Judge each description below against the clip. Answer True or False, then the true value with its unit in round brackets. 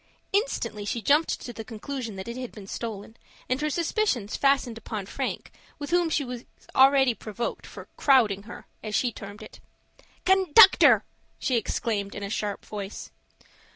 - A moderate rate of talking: True (160 wpm)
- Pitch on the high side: True (235 Hz)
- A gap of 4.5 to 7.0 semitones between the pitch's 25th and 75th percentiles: True (5.1 semitones)